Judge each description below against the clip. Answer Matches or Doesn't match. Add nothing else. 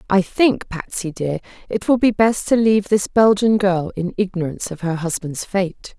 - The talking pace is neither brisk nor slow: Matches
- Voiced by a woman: Matches